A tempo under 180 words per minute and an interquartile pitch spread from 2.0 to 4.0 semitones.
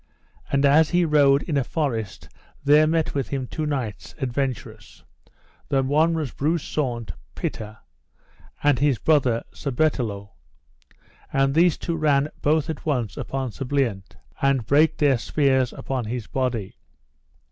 Yes: average, 145 wpm; average, 3.7 semitones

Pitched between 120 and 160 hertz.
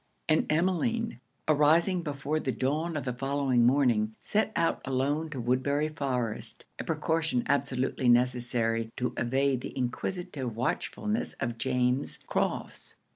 Yes: low, 135 Hz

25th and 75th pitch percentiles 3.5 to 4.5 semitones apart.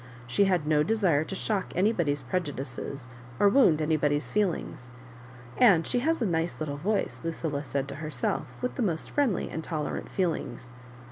No: wide, 5.4 semitones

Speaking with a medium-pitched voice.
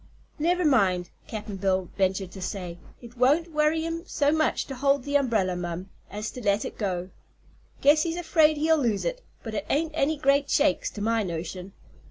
No: high, 245 Hz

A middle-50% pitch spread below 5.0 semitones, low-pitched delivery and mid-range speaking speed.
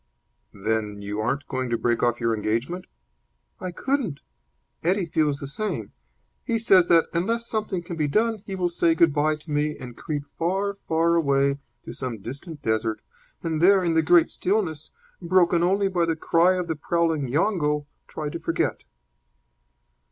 No: average, 4.5 semitones; medium, 165 Hz; average, 170 wpm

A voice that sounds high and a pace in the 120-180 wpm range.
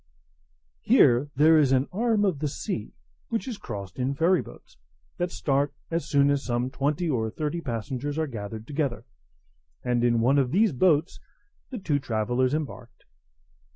No: medium, 140 Hz; average, 160 wpm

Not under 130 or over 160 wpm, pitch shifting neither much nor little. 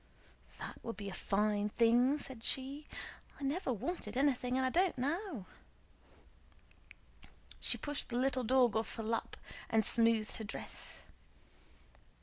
Yes: slow, 135 wpm; average, 3.7 semitones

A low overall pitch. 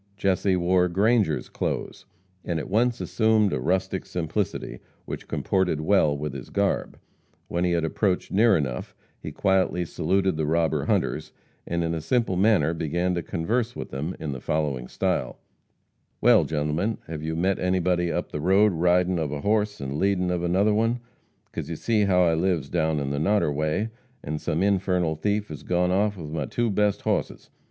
Yes: very low, 90 Hz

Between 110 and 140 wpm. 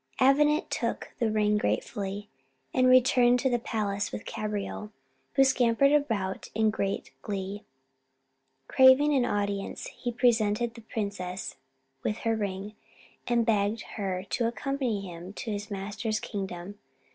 Yes: slow, 135 wpm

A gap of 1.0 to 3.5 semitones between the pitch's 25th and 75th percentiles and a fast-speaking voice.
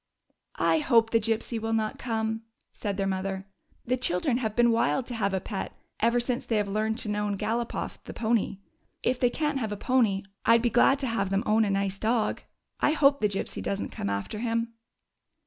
Yes: average, 2.9 semitones; fast, 220 wpm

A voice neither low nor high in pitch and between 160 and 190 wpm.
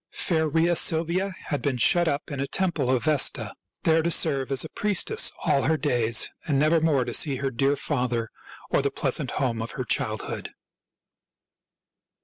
Yes: medium, 145 Hz; average, 170 wpm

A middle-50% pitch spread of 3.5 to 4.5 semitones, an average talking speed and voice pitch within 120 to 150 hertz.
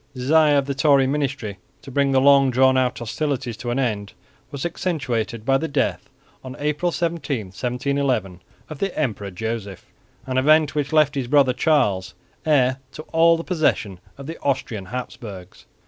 Yes: average, 3.9 semitones; average, 170 wpm; low, 135 Hz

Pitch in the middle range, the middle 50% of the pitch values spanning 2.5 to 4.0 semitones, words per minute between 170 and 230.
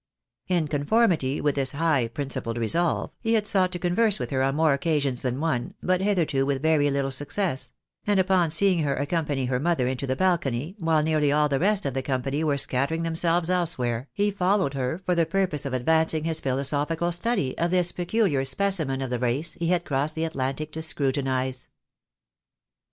No: medium, 155 Hz; average, 4.5 semitones; average, 185 wpm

